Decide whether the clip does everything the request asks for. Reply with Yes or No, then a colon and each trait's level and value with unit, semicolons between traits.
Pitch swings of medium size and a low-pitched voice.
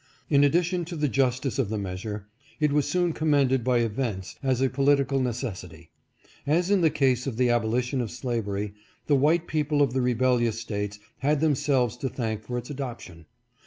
Yes: average, 3.7 semitones; low, 130 Hz